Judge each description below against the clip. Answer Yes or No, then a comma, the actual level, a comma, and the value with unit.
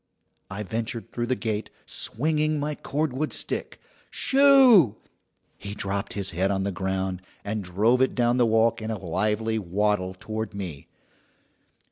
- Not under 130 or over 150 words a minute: Yes, average, 145 wpm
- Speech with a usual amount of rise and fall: Yes, average, 4.3 semitones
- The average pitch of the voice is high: No, low, 110 Hz